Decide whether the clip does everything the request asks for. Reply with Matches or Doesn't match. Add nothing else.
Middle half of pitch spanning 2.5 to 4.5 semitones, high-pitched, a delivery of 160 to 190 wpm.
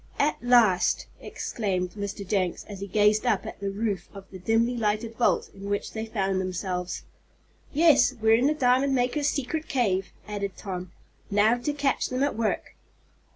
Matches